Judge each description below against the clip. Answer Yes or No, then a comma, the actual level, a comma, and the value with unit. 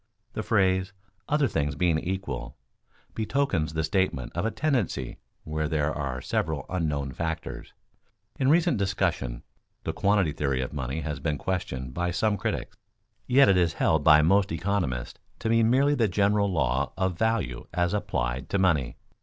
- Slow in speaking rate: No, average, 160 wpm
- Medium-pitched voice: No, very low, 85 Hz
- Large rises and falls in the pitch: Yes, wide, 5.8 semitones